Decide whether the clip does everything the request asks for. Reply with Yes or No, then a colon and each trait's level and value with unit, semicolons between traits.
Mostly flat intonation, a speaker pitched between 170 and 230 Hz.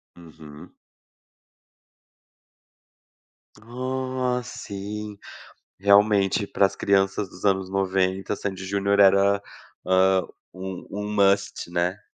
No: narrow, 1.5 semitones; low, 100 Hz